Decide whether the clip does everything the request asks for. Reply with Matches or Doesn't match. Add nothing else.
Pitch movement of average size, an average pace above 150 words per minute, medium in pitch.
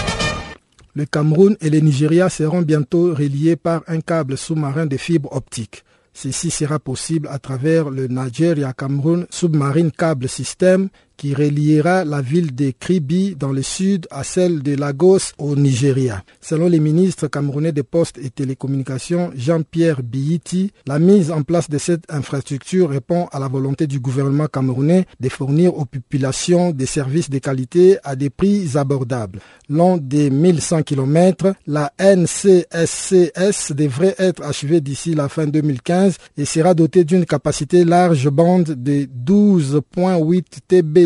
Doesn't match